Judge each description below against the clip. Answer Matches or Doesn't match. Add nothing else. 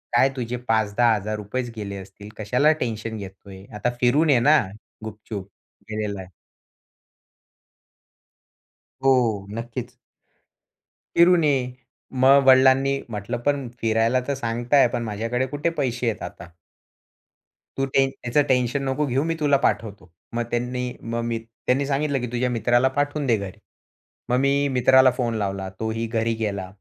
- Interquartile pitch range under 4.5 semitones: Matches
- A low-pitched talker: Matches